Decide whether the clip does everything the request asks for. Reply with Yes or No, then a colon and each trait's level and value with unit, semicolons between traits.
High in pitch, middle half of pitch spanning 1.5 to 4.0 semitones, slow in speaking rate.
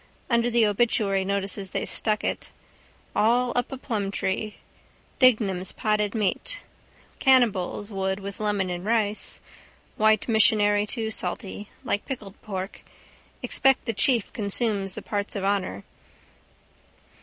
Yes: high, 210 Hz; narrow, 2.6 semitones; slow, 120 wpm